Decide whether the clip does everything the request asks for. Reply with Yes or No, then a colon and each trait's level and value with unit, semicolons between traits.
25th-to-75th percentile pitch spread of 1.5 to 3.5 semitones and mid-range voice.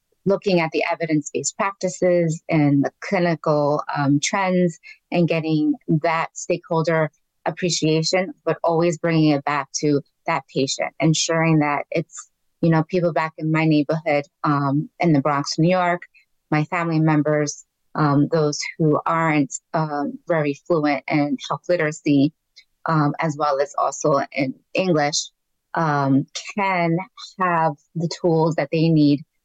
Yes: narrow, 2.5 semitones; medium, 160 Hz